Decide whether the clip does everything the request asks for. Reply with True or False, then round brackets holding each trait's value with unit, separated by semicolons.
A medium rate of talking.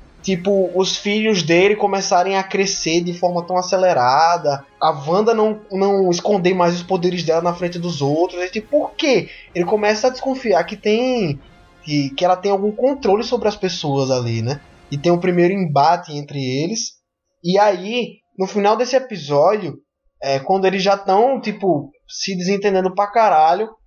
True (175 wpm)